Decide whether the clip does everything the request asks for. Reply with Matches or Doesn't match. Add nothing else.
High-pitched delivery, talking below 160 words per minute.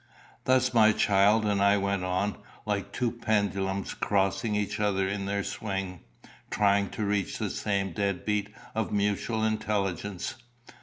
Doesn't match